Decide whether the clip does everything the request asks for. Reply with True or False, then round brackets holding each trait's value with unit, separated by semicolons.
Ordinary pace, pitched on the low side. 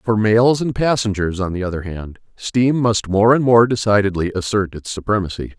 True (185 wpm; 105 Hz)